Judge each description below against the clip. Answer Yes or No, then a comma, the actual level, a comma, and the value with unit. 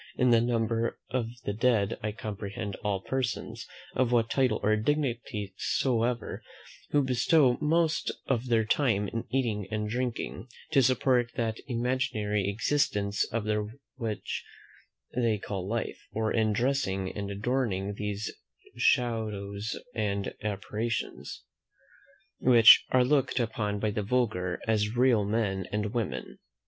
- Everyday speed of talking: No, slow, 130 wpm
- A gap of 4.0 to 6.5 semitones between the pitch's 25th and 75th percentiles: No, average, 3.2 semitones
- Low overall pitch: Yes, low, 110 Hz